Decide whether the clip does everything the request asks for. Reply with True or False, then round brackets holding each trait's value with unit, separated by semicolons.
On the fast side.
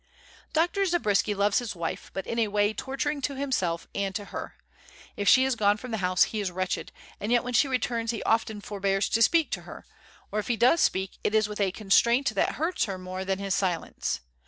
True (225 wpm)